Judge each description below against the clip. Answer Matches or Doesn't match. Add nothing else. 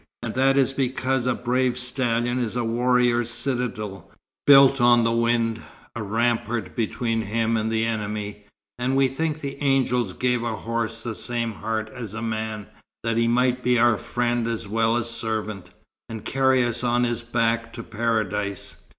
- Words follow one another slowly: Doesn't match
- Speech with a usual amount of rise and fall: Doesn't match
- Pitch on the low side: Matches